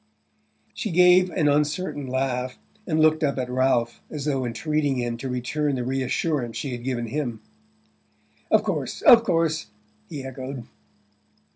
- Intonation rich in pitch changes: No, average, 3.6 semitones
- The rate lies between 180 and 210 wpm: No, average, 145 wpm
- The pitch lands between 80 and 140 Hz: Yes, low, 135 Hz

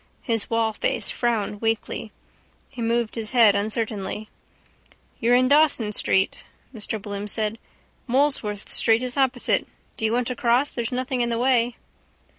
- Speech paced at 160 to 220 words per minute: No, average, 145 wpm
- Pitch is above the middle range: Yes, high, 230 Hz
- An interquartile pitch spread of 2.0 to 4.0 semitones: Yes, narrow, 2.4 semitones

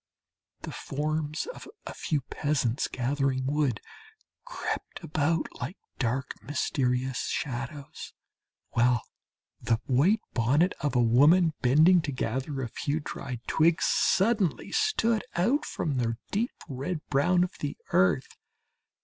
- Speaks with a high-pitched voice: No, medium, 145 Hz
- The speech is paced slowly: Yes, slow, 125 wpm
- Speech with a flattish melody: No, average, 4.6 semitones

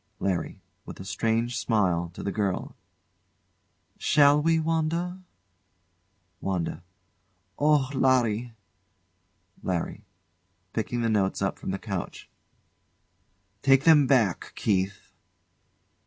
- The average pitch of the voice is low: Yes, low, 115 Hz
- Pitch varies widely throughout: Yes, wide, 6.7 semitones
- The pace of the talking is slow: Yes, slow, 95 wpm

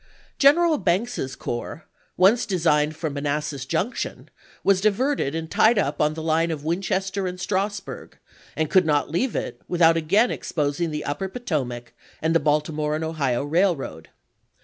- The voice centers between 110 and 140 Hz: No, medium, 165 Hz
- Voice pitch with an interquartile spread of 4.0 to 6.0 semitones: Yes, average, 4.5 semitones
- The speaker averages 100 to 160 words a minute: Yes, average, 155 wpm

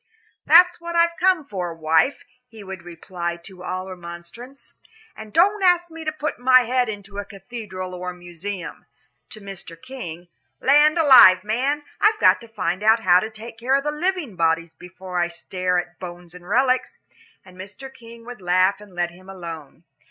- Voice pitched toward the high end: Yes, high, 200 Hz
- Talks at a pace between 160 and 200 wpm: Yes, average, 180 wpm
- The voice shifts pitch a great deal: Yes, wide, 6.8 semitones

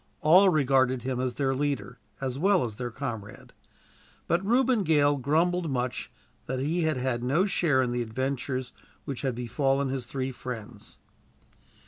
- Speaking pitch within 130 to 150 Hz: Yes, low, 135 Hz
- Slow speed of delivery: No, average, 155 wpm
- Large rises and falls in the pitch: No, average, 3.7 semitones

